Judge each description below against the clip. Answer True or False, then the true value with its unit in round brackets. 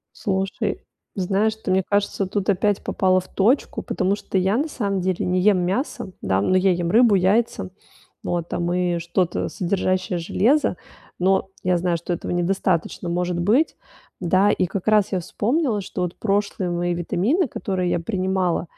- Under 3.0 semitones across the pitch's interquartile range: True (2.4 semitones)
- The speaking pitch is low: False (185 Hz)